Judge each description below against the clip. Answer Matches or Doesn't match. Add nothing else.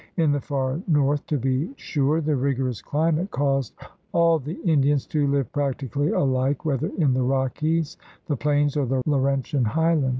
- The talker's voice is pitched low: Doesn't match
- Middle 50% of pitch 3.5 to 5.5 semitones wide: Doesn't match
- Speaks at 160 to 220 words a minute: Matches